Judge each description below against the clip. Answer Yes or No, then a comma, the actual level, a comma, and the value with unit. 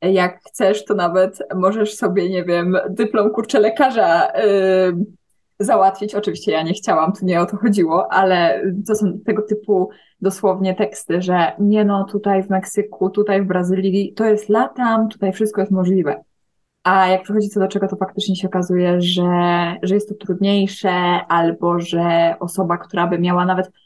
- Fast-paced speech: Yes, fast, 170 wpm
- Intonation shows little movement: Yes, narrow, 2.3 semitones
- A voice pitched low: No, high, 190 Hz